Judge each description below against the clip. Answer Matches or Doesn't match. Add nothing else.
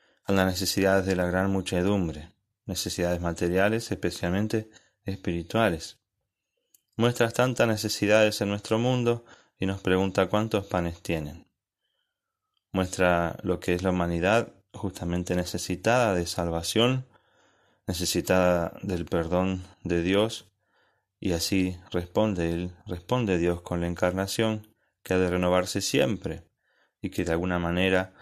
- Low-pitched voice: Matches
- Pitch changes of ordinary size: Matches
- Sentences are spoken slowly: Matches